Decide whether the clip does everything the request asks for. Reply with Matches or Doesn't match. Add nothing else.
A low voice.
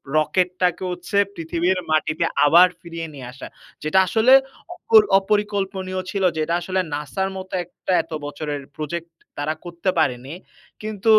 Doesn't match